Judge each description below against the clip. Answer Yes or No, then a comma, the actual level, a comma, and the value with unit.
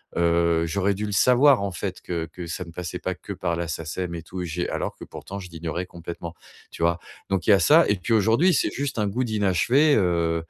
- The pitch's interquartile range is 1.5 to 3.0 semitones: No, average, 3.7 semitones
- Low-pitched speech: Yes, very low, 90 Hz